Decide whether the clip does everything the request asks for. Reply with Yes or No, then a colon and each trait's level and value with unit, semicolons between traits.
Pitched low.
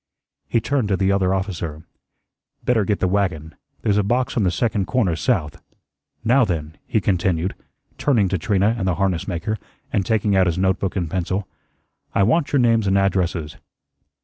Yes: very low, 95 Hz